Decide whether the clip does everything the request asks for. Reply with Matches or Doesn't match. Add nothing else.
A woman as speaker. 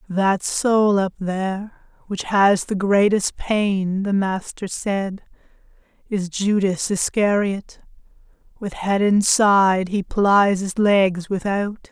Matches